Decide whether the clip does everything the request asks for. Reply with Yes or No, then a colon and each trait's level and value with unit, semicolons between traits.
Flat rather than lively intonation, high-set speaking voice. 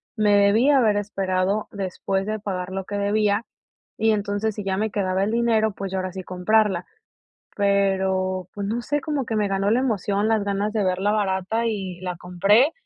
Yes: narrow, 2.2 semitones; high, 200 Hz